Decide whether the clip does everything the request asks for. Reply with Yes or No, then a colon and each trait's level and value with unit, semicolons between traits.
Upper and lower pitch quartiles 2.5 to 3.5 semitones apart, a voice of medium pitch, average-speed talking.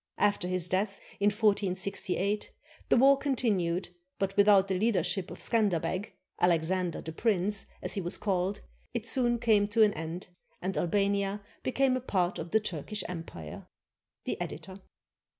No: average, 2.9 semitones; high, 195 Hz; average, 150 wpm